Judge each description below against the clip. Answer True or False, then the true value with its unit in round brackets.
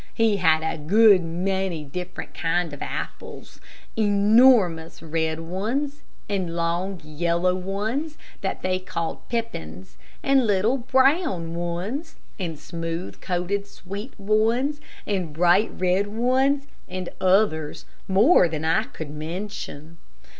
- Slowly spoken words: True (120 wpm)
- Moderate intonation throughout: True (4.7 semitones)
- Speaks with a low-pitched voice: False (185 Hz)